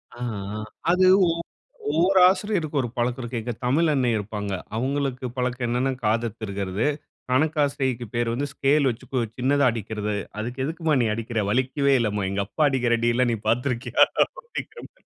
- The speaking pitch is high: No, low, 125 Hz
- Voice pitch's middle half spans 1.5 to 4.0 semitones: Yes, average, 3.7 semitones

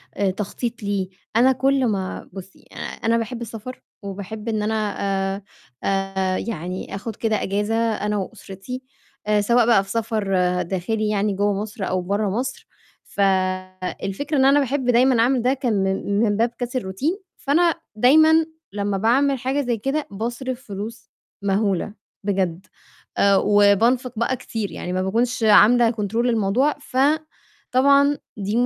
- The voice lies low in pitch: No, high, 220 Hz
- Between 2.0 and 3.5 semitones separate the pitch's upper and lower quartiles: No, average, 4.1 semitones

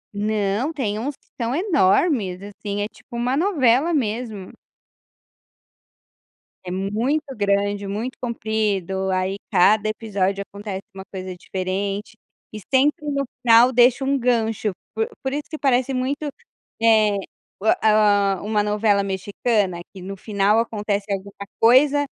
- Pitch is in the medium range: No, high, 215 Hz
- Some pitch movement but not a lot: Yes, average, 3.9 semitones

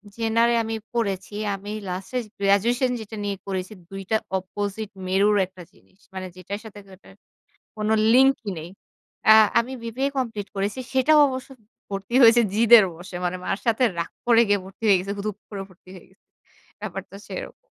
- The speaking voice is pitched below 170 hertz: No, high, 205 Hz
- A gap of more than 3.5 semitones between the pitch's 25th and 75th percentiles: No, average, 3.2 semitones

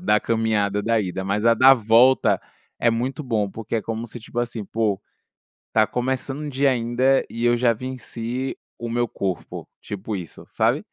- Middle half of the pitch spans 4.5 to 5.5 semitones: No, narrow, 2.6 semitones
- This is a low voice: Yes, low, 115 Hz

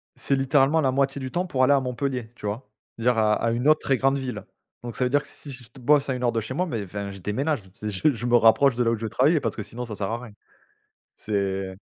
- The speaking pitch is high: No, low, 125 Hz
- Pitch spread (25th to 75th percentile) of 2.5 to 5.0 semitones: Yes, average, 3.8 semitones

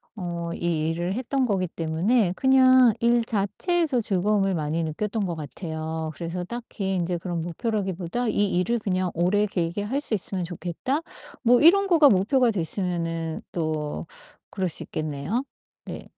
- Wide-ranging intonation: Yes, wide, 5.8 semitones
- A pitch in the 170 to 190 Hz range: Yes, medium, 185 Hz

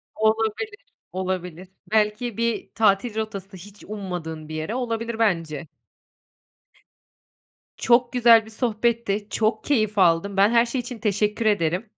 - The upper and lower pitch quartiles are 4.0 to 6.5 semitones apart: No, average, 3.6 semitones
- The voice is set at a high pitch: Yes, high, 215 Hz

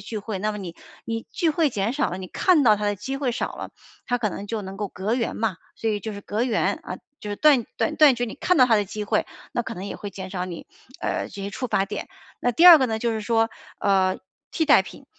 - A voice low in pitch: No, high, 220 Hz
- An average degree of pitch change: Yes, average, 3.4 semitones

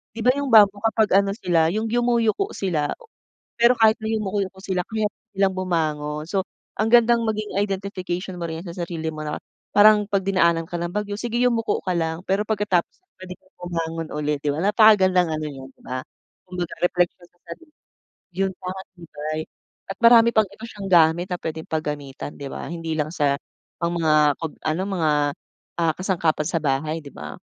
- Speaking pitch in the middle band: Yes, medium, 180 Hz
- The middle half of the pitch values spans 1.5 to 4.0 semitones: No, average, 4.5 semitones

